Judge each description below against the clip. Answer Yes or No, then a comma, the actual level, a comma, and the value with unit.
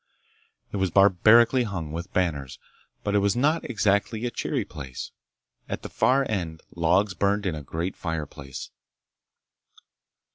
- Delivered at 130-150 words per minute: Yes, average, 140 wpm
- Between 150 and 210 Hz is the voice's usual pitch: No, very low, 95 Hz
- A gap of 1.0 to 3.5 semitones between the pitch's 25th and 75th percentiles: No, average, 4.8 semitones